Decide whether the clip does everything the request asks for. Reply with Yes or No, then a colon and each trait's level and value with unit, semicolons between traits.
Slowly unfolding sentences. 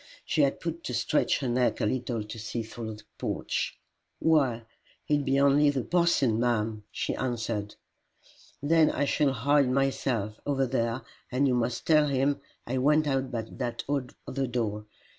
No: average, 165 wpm